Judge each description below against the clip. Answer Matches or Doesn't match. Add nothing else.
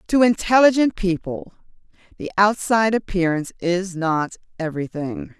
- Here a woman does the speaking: Matches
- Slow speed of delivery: Matches